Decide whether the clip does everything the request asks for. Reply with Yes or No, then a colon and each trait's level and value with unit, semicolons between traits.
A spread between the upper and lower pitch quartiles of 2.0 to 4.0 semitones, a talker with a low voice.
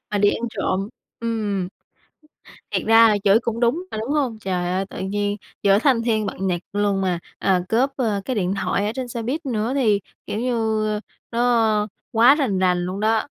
No: average, 2.9 semitones; high, 215 Hz